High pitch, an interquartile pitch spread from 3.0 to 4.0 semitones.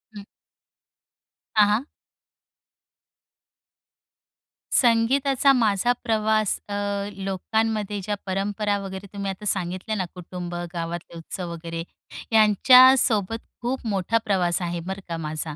Yes: high, 200 Hz; average, 3.6 semitones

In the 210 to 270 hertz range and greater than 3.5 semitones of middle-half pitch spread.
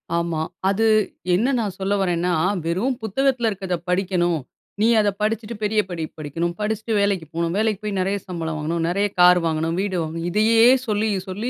No: high, 190 Hz; average, 4.1 semitones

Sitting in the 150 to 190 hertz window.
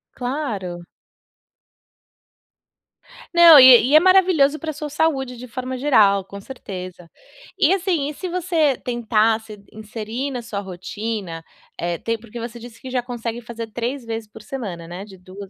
No: high, 235 Hz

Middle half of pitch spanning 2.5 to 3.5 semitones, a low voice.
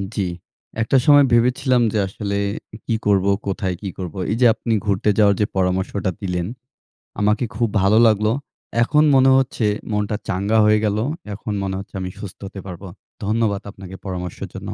Yes: average, 2.8 semitones; low, 100 Hz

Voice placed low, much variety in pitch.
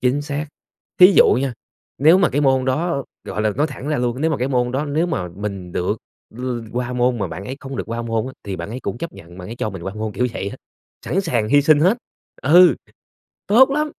Yes: low, 130 Hz; wide, 5.7 semitones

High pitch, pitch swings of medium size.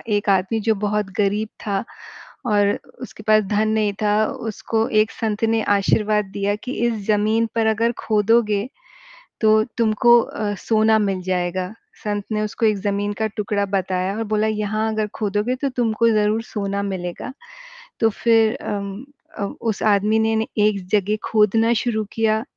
No: high, 215 Hz; narrow, 1.4 semitones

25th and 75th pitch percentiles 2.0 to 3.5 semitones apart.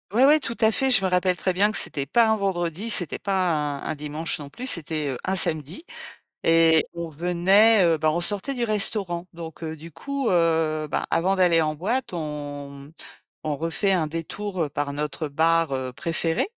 No: average, 4.1 semitones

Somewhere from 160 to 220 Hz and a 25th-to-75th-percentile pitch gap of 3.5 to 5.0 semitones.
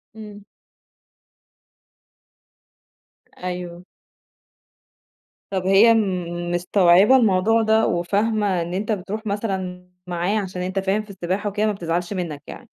No: high, 190 Hz; average, 2.8 semitones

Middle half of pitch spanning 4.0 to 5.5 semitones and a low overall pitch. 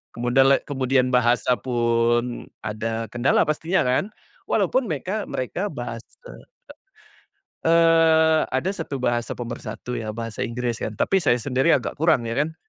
Yes: average, 4.5 semitones; low, 125 Hz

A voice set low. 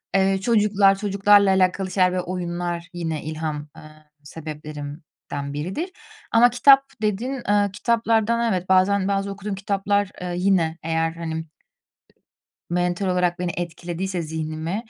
No: medium, 185 Hz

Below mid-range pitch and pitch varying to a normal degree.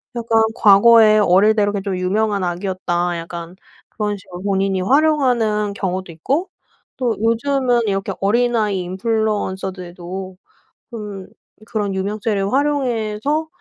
No: high, 205 Hz; average, 3.5 semitones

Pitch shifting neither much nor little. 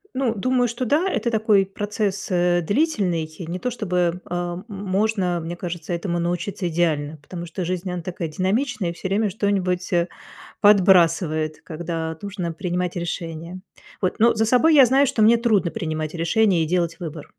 Yes: average, 3.7 semitones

